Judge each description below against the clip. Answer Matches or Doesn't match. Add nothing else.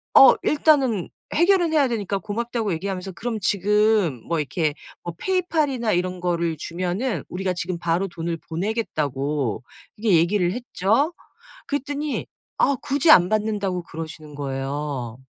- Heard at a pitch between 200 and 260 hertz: Doesn't match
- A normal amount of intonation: Doesn't match